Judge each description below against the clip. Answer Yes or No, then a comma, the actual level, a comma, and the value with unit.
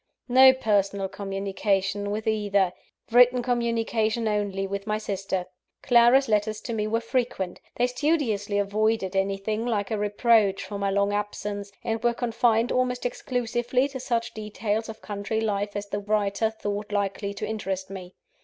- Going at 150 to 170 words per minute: Yes, average, 155 wpm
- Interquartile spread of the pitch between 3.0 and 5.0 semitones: No, narrow, 2.6 semitones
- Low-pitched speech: No, high, 210 Hz